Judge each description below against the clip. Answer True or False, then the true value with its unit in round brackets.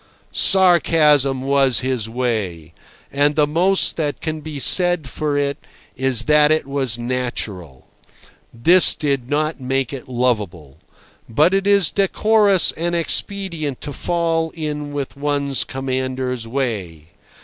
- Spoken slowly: True (125 wpm)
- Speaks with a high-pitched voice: False (140 Hz)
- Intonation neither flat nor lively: True (3.9 semitones)